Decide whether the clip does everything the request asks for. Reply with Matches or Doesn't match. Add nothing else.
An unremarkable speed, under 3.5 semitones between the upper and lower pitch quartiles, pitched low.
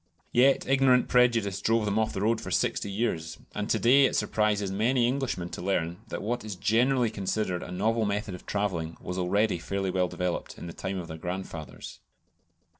Doesn't match